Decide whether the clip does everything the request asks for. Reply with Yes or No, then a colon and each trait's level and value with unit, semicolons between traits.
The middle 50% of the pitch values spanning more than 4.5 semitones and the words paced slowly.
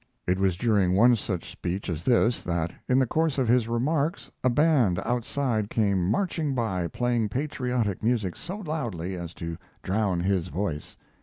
No: wide, 5.6 semitones; average, 165 wpm